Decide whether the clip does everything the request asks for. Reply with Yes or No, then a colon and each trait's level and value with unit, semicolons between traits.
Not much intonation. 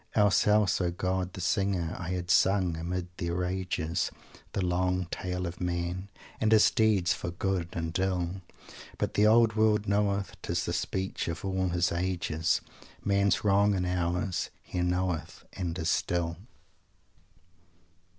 Yes: narrow, 2.0 semitones